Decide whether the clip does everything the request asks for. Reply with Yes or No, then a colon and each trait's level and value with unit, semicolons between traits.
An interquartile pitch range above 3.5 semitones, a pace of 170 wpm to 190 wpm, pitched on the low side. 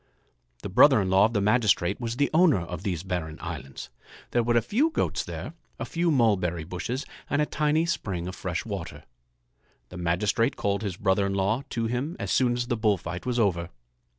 No: average, 5.1 semitones; fast, 205 wpm; low, 105 Hz